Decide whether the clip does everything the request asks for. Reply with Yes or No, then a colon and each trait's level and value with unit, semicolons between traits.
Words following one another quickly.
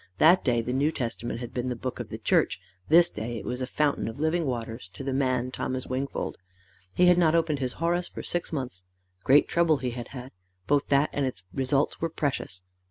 Yes: fast, 220 wpm